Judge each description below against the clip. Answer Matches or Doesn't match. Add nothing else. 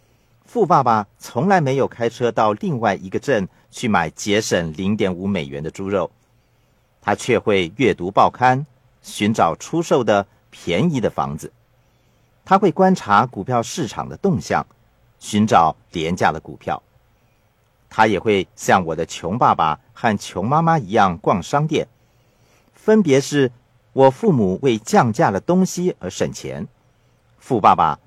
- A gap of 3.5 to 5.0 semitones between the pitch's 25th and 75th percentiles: Doesn't match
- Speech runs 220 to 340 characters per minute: Doesn't match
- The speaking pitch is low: Matches